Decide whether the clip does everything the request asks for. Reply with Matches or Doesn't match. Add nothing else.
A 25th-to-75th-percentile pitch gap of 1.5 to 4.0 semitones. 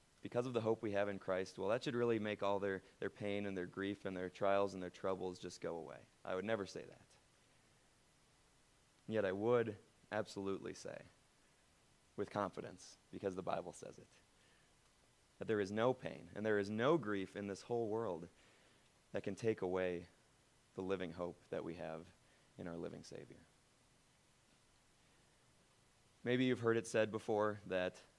Matches